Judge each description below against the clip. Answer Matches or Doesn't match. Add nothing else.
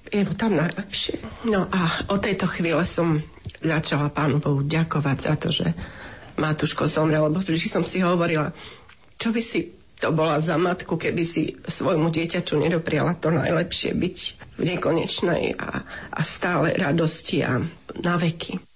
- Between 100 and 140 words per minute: Doesn't match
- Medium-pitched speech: Matches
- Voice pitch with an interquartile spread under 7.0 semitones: Matches